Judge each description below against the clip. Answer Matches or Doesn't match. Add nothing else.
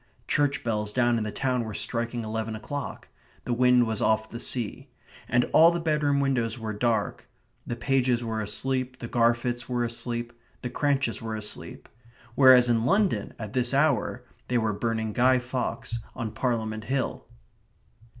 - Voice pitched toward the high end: Doesn't match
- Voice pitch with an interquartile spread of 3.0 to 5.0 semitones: Doesn't match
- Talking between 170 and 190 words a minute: Doesn't match